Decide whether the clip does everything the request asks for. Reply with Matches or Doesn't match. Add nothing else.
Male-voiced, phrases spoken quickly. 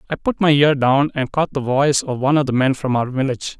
Matches